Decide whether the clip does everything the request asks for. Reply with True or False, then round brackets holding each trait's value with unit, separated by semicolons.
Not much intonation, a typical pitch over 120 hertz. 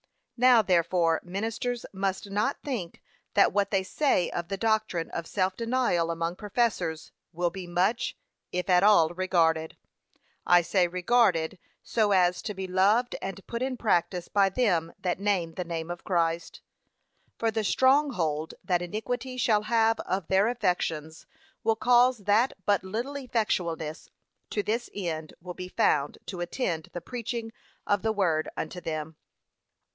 False (4.6 semitones; 190 Hz)